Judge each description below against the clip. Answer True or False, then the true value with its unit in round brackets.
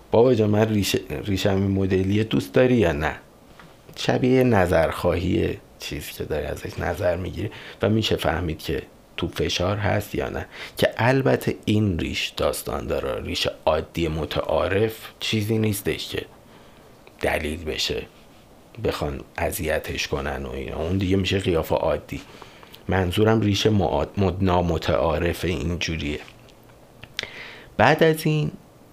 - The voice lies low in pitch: True (95 Hz)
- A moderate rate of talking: True (125 wpm)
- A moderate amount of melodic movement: True (4.0 semitones)